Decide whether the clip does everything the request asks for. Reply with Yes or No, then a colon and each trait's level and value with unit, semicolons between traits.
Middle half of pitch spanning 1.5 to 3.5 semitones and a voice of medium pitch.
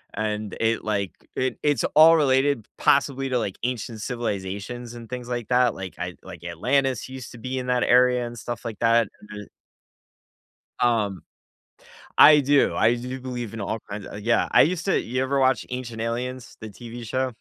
No: average, 2.8 semitones; low, 120 Hz